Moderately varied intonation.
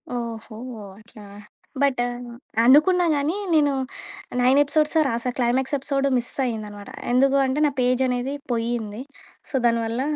Yes: average, 3.3 semitones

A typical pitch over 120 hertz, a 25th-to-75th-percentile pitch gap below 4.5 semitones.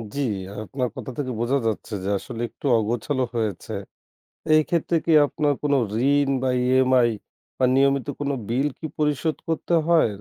Yes: low, 135 Hz; average, 3.0 semitones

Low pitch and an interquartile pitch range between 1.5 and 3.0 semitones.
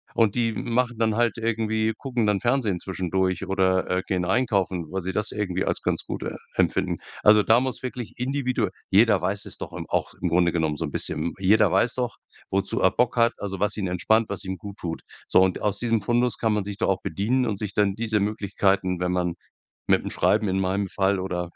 No: low, 100 Hz; average, 3.4 semitones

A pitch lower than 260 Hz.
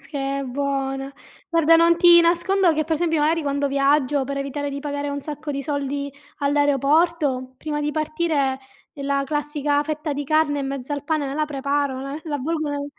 No: very high, 290 Hz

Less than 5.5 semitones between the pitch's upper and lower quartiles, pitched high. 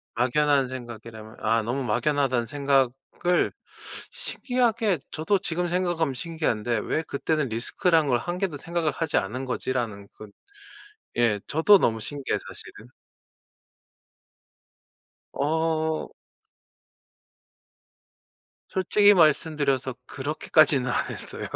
No: average, 5.1 semitones; medium, 145 Hz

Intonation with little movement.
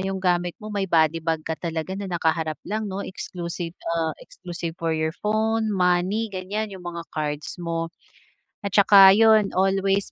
No: average, 3.3 semitones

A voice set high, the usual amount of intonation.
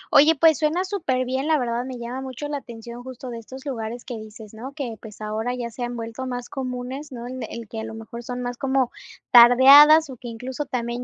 No: very high, 250 Hz; narrow, 2.2 semitones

